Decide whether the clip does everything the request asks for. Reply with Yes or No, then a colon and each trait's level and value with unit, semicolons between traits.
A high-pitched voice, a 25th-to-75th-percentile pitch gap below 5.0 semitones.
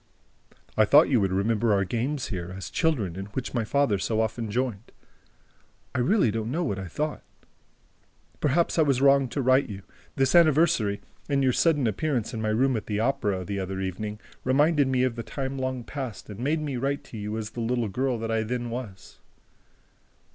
No: low, 120 Hz; average, 4.5 semitones